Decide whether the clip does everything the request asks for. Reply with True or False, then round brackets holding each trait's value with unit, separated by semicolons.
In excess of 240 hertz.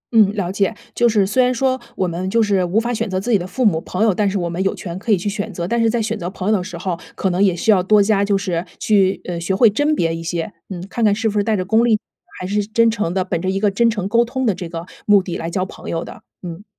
False (200 Hz)